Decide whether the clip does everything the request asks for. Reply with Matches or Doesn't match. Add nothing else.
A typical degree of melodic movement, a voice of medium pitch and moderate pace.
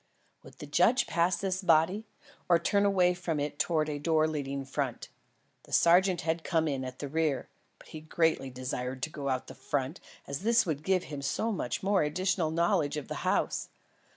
Matches